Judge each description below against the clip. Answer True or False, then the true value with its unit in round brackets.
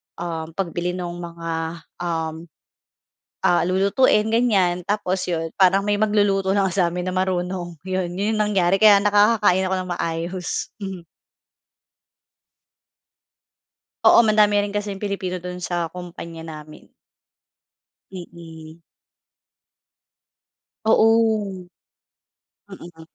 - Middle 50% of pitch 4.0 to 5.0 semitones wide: False (2.9 semitones)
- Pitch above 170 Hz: True (185 Hz)